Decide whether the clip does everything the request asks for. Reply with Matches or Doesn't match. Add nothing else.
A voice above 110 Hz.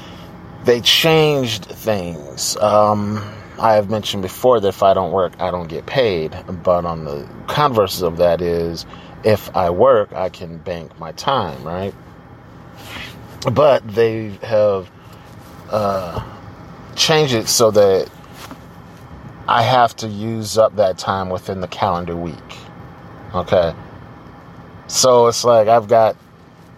Doesn't match